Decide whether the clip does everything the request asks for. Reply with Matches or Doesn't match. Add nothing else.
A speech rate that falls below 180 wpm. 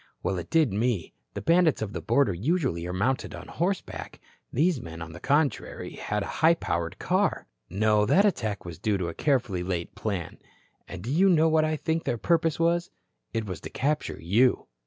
Doesn't match